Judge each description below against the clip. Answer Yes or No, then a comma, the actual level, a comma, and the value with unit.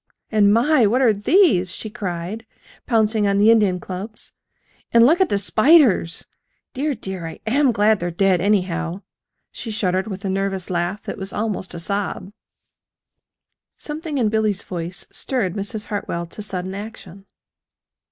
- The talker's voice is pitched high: Yes, high, 205 Hz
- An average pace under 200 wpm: Yes, average, 150 wpm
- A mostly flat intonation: No, average, 3.3 semitones